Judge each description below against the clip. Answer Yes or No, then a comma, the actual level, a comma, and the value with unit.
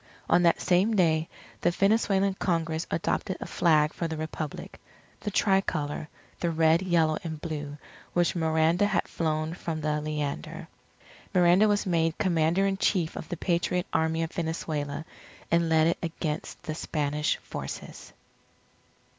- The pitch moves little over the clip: Yes, narrow, 2.2 semitones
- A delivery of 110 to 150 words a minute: Yes, average, 145 wpm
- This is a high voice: No, medium, 165 Hz